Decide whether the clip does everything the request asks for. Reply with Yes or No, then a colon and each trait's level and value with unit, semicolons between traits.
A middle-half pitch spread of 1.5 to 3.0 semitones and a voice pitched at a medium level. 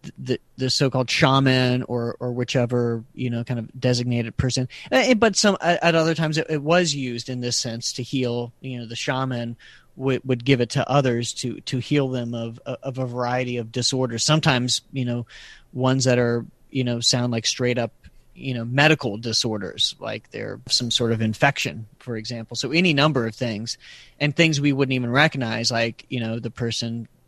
No: narrow, 2.5 semitones; low, 125 Hz